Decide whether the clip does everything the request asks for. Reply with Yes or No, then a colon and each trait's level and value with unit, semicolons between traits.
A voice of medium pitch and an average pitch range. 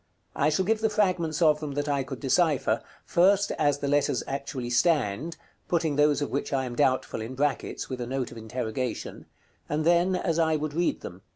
Yes: medium, 145 Hz; average, 4.1 semitones